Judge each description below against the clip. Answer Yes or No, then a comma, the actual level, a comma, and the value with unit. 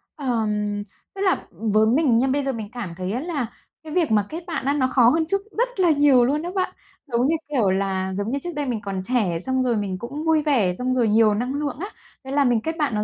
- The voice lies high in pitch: Yes, very high, 255 Hz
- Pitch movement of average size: No, wide, 5.7 semitones